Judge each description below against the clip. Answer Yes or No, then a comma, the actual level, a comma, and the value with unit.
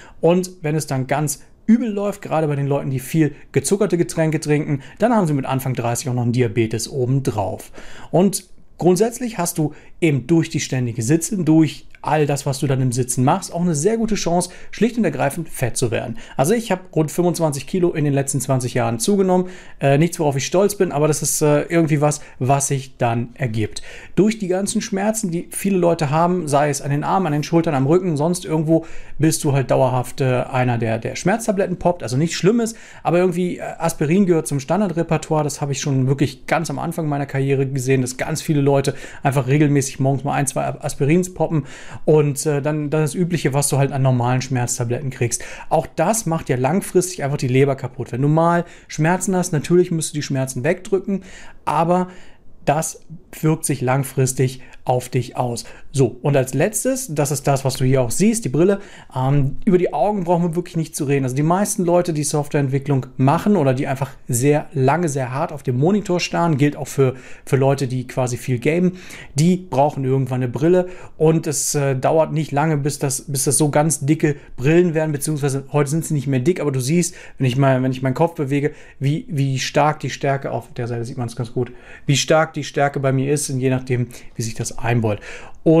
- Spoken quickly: Yes, fast, 210 wpm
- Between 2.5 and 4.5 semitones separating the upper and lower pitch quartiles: Yes, average, 4.1 semitones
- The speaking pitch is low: No, medium, 150 Hz